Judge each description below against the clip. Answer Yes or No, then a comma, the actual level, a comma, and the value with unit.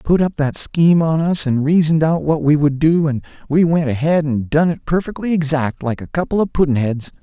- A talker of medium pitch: Yes, medium, 155 Hz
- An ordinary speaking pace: No, fast, 230 wpm